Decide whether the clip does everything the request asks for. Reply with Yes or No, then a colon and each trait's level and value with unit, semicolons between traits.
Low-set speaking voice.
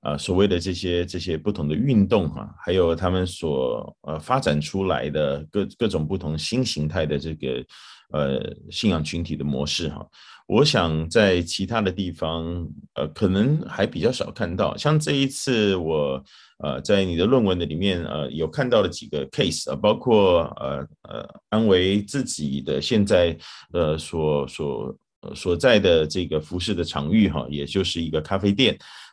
Yes: very low, 85 Hz